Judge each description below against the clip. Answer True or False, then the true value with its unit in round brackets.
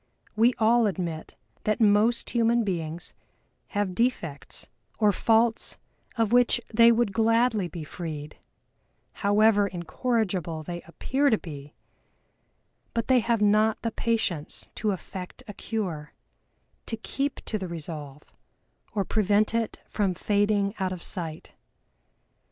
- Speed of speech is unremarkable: False (125 wpm)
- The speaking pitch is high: True (205 Hz)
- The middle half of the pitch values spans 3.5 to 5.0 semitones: True (4.7 semitones)